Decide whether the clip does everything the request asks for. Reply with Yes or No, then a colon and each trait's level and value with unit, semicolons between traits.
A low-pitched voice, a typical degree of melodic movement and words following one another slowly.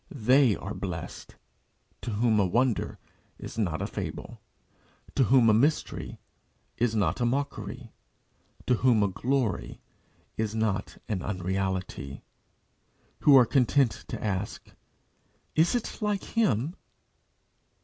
Yes: low, 115 Hz; average, 4.7 semitones; slow, 120 wpm